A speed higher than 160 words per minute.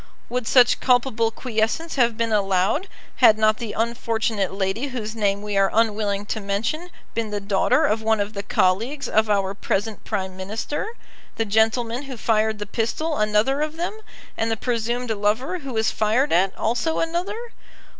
Yes: average, 170 wpm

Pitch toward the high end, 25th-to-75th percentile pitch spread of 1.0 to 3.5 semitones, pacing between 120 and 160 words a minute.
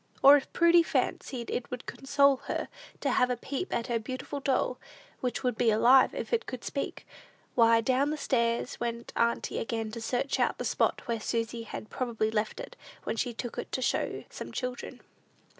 No: high, 245 Hz; average, 2.7 semitones; average, 190 wpm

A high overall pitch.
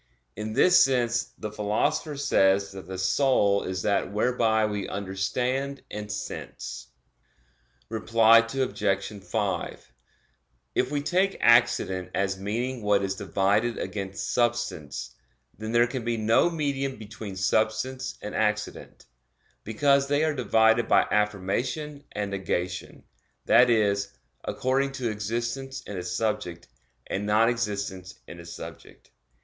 No: low, 110 Hz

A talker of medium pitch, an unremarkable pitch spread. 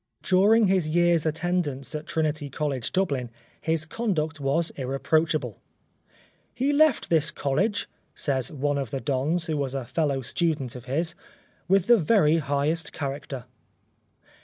Yes: medium, 155 Hz; average, 3.9 semitones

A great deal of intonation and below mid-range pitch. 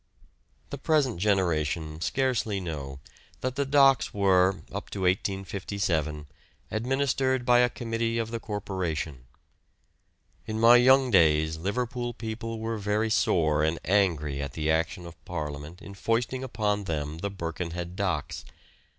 Yes: wide, 6.1 semitones; low, 100 Hz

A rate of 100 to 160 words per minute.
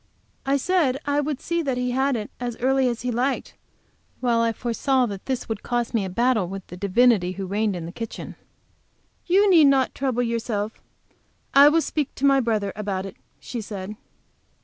No: average, 195 wpm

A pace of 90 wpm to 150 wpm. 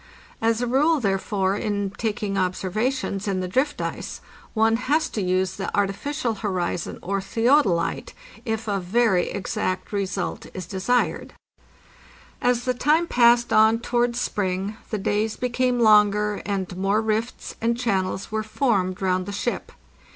Yes: average, 145 wpm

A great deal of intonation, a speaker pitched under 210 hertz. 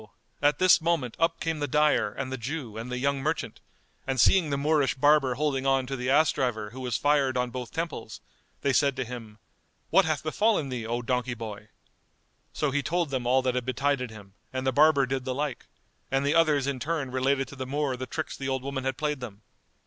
No: average, 2.9 semitones; low, 135 Hz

